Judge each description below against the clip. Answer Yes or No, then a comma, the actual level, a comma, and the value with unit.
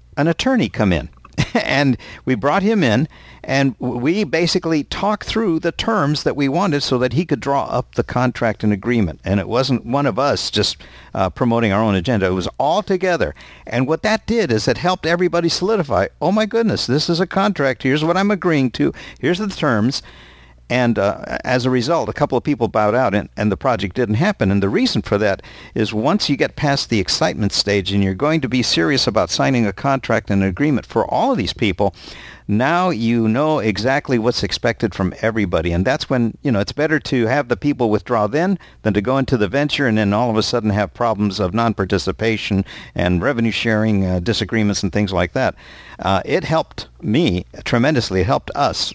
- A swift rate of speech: Yes, fast, 210 wpm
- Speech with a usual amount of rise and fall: No, wide, 6.0 semitones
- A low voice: Yes, low, 125 Hz